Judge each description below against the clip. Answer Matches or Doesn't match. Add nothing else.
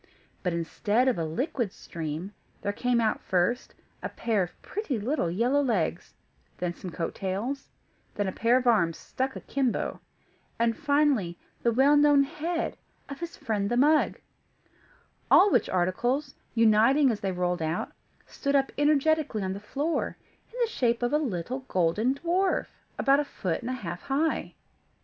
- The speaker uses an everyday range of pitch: Doesn't match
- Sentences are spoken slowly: Doesn't match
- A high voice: Matches